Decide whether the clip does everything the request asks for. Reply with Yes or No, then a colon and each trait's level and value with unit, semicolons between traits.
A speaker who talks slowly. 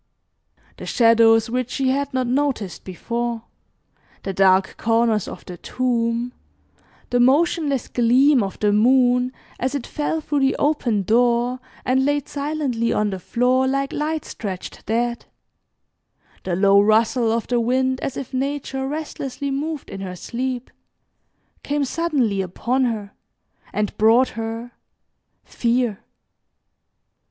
Yes: slow, 130 wpm